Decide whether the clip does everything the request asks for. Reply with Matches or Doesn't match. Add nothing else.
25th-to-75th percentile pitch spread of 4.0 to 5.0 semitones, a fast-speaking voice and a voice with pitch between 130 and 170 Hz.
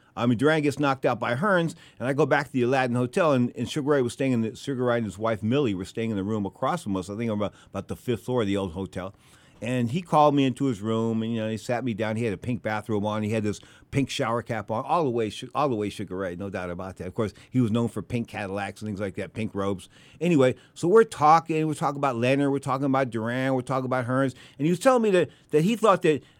Doesn't match